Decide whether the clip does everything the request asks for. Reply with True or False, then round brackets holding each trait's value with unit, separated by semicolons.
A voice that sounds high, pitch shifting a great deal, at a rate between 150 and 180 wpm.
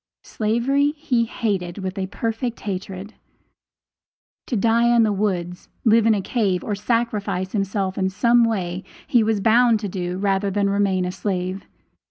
False (205 Hz; 3.4 semitones; 160 wpm)